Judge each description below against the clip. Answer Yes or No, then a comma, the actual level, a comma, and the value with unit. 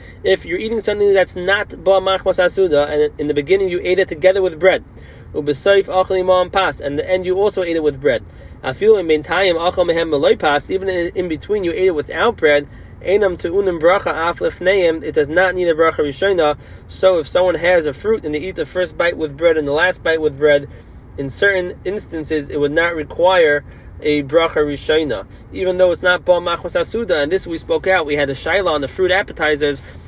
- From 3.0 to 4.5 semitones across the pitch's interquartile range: Yes, average, 4.0 semitones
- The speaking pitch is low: No, medium, 170 Hz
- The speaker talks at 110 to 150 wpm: No, average, 185 wpm